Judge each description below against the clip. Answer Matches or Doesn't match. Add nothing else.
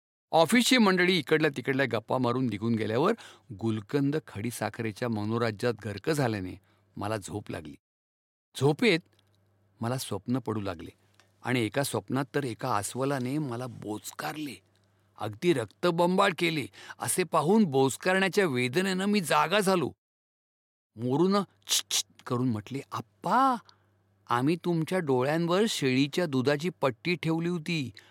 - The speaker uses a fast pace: Doesn't match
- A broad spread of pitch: Matches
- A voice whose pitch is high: Doesn't match